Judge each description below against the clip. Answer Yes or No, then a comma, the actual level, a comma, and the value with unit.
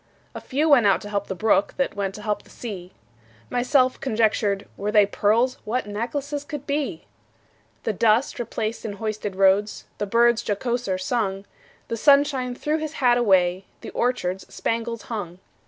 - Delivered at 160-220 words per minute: Yes, average, 165 wpm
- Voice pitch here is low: No, high, 220 Hz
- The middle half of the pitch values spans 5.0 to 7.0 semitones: No, average, 3.7 semitones